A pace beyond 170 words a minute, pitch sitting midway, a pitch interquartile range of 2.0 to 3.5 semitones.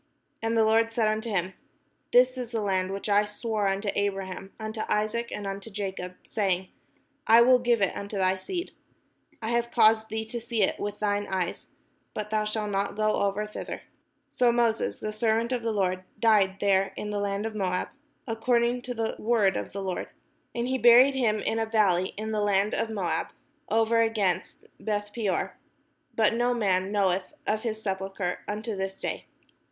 No: average, 185 wpm; high, 215 Hz; narrow, 2.6 semitones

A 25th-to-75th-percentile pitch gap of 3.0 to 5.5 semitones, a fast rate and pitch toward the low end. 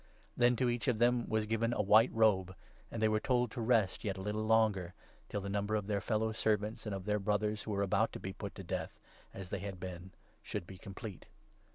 No: narrow, 2.4 semitones; fast, 245 wpm; low, 105 Hz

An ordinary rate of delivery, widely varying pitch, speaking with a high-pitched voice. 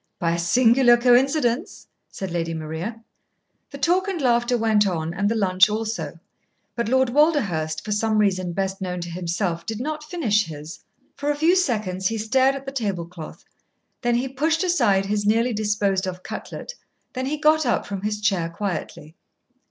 Yes: average, 175 wpm; wide, 6.1 semitones; high, 215 Hz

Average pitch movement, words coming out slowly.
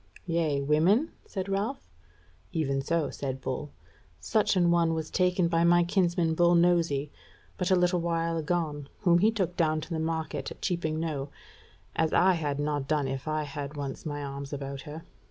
No: average, 3.1 semitones; average, 180 wpm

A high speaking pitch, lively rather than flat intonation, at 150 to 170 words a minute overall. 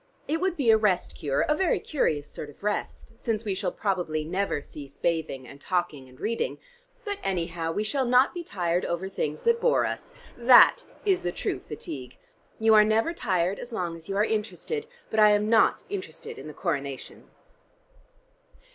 No: high, 200 Hz; wide, 6.4 semitones; average, 185 wpm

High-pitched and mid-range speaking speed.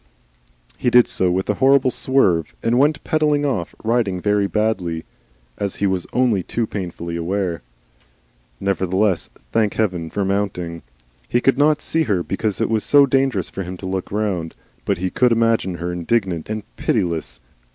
No: low, 100 Hz; average, 170 wpm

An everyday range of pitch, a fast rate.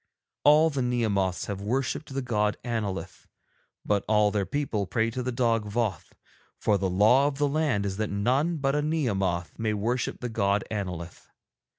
No: average, 4.7 semitones; average, 175 wpm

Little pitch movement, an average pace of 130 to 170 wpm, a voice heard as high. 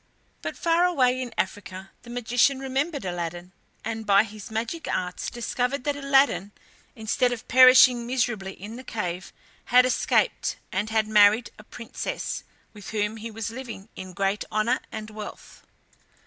No: average, 3.7 semitones; average, 150 wpm; high, 225 Hz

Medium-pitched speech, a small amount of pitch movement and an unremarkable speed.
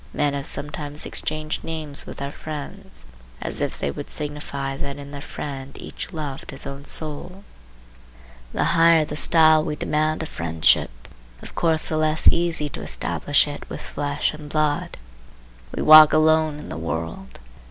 Yes: medium, 150 Hz; narrow, 1.8 semitones; average, 165 wpm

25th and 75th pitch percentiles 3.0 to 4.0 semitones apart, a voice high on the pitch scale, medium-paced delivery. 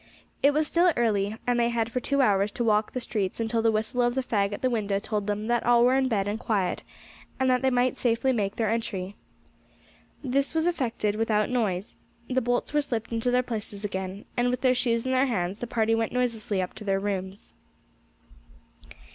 No: average, 3.3 semitones; high, 230 Hz; fast, 210 wpm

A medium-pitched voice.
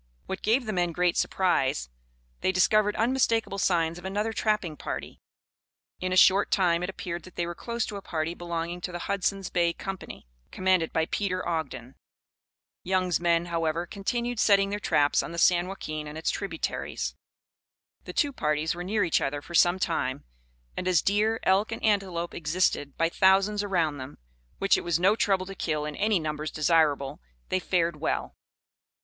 Yes: medium, 180 Hz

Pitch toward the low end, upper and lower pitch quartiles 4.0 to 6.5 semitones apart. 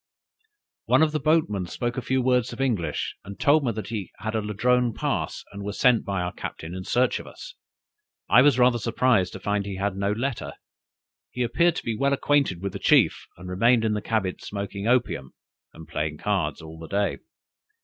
Yes: low, 105 Hz; average, 4.5 semitones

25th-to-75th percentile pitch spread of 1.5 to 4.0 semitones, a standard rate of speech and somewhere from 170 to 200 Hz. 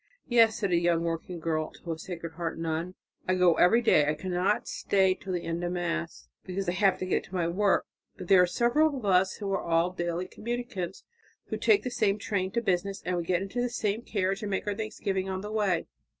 No: average, 3.1 semitones; fast, 235 wpm; medium, 185 Hz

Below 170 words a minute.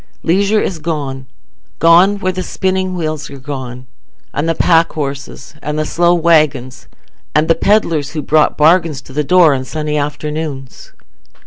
Yes: average, 150 wpm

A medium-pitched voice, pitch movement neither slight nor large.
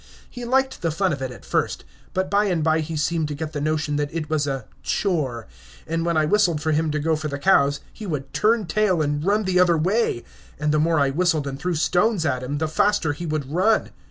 Yes: medium, 160 Hz; average, 3.7 semitones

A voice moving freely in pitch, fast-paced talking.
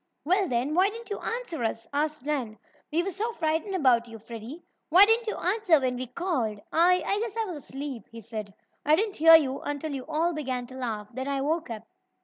Yes: wide, 6.4 semitones; fast, 220 wpm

